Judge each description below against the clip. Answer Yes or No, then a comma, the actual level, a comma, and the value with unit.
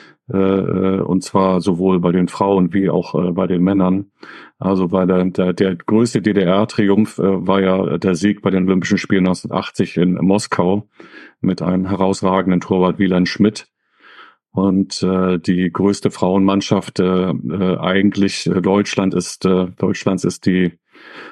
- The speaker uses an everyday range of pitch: No, narrow, 1.1 semitones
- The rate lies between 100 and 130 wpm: Yes, slow, 125 wpm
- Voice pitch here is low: Yes, very low, 95 Hz